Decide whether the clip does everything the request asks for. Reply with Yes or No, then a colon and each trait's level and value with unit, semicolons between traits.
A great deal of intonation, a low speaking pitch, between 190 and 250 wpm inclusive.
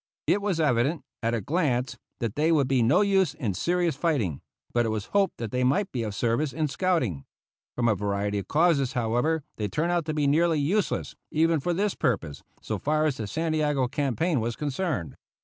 No: wide, 5.9 semitones; medium, 145 Hz; average, 200 wpm